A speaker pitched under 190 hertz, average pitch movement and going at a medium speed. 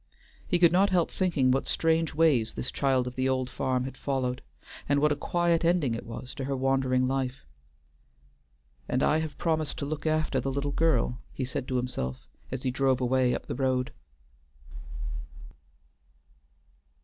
Yes: low, 135 Hz; average, 3.4 semitones; average, 170 wpm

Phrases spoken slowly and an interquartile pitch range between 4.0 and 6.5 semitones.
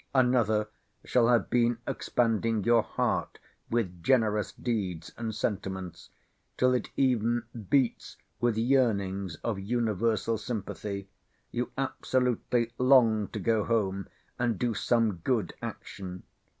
No: slow, 115 wpm; average, 3.3 semitones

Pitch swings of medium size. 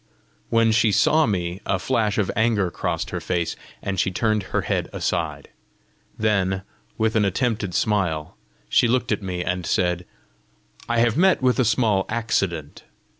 Yes: average, 3.8 semitones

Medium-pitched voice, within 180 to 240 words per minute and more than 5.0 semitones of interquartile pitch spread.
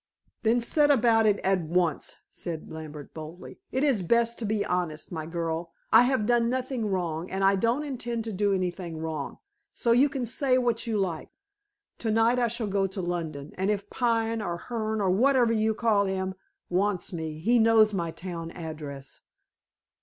No: high, 200 Hz; average, 185 wpm; wide, 5.4 semitones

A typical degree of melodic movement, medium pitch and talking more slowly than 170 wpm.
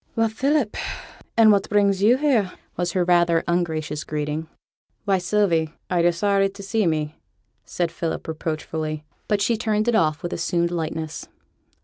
Yes: average, 4.4 semitones; medium, 175 Hz; average, 155 wpm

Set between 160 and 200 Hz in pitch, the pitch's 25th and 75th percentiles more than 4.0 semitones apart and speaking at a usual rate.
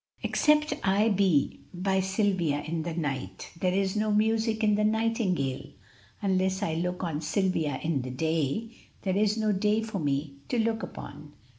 Yes: high, 190 Hz; average, 5.1 semitones; average, 165 wpm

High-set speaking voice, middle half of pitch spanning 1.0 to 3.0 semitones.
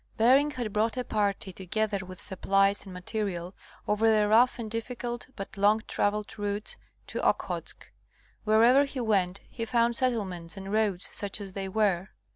Yes: high, 210 Hz; average, 2.7 semitones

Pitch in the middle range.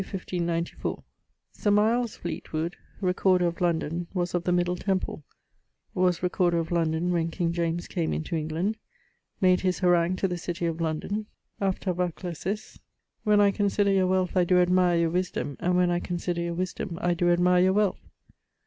Yes: medium, 180 Hz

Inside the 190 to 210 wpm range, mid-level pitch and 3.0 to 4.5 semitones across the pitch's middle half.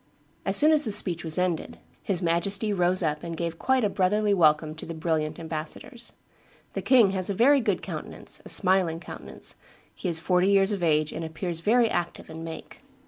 Yes: average, 195 wpm; medium, 180 Hz; average, 3.7 semitones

